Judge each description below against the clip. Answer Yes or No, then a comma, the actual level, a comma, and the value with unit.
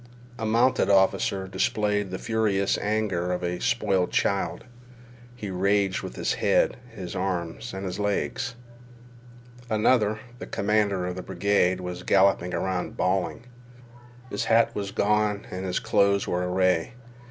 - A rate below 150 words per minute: Yes, average, 140 wpm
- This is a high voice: No, low, 100 Hz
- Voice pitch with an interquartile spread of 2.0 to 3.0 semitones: Yes, narrow, 2.5 semitones